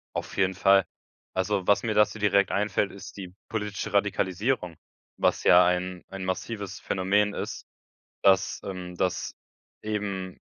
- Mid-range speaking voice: No, very low, 95 Hz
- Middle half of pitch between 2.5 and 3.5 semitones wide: No, narrow, 1.9 semitones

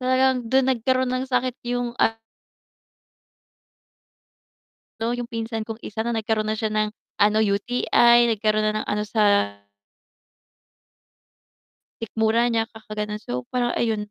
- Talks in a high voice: Yes, high, 225 Hz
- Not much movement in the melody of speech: Yes, narrow, 2.3 semitones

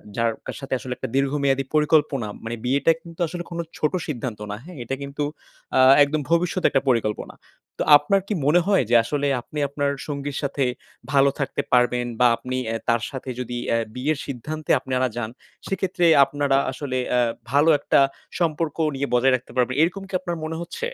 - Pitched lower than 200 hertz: Yes, medium, 140 Hz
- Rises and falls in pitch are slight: No, average, 3.5 semitones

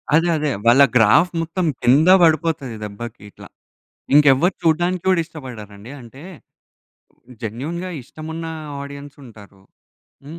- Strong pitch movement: Yes, wide, 5.7 semitones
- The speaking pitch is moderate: Yes, medium, 145 Hz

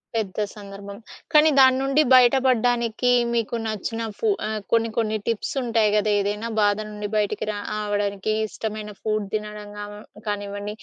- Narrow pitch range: Yes, narrow, 1.9 semitones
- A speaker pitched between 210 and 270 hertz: Yes, high, 215 Hz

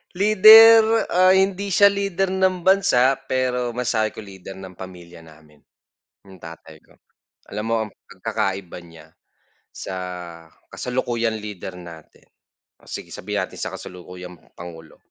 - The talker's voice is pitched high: No, low, 115 Hz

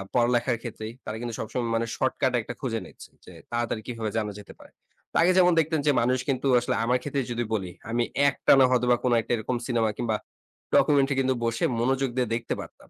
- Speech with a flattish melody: Yes, narrow, 2.2 semitones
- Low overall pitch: Yes, low, 120 Hz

